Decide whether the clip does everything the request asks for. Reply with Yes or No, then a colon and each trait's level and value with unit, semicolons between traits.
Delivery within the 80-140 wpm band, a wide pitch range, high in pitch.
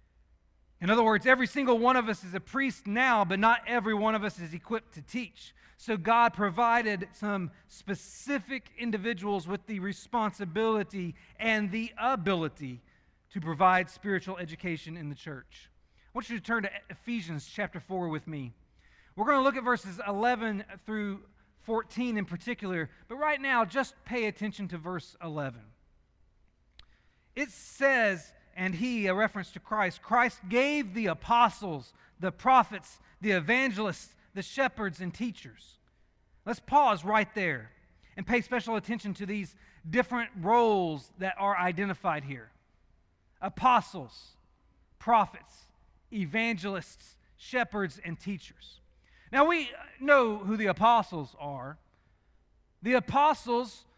Yes: slow, 135 wpm; wide, 5.7 semitones; high, 200 Hz